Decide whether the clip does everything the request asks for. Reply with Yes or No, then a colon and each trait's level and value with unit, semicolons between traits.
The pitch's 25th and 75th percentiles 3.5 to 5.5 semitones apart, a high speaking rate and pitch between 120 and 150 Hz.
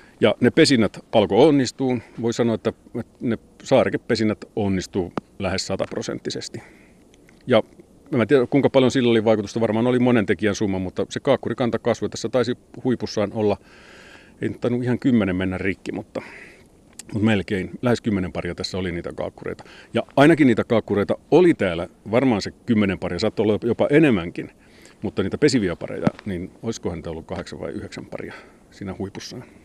No: average, 4.0 semitones; fast, 160 wpm; low, 110 Hz